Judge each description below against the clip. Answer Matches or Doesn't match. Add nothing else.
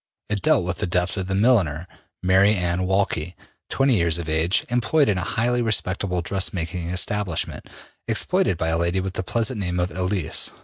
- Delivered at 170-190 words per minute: Matches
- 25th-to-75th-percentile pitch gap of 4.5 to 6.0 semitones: Doesn't match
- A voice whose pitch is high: Doesn't match